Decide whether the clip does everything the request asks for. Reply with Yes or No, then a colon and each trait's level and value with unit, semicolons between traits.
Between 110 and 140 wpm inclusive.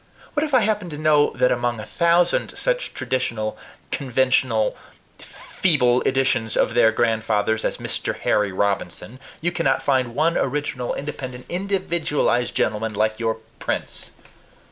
Yes: slow, 135 wpm